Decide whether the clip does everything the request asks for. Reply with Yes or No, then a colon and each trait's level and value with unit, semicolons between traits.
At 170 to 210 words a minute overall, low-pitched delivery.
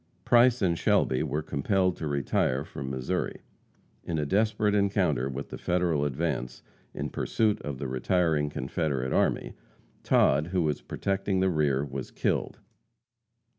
No: average, 140 wpm; very low, 75 Hz